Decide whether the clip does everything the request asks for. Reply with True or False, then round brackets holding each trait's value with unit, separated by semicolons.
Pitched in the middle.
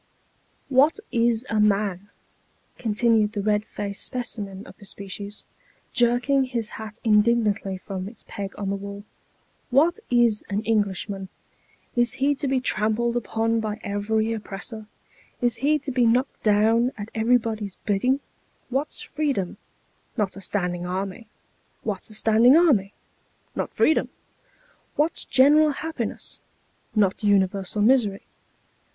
False (220 Hz)